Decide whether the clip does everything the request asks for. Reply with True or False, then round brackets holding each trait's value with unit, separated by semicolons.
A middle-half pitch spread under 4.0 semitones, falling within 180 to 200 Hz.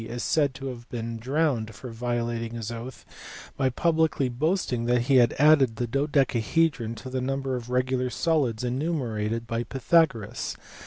False (3.0 semitones; 125 Hz)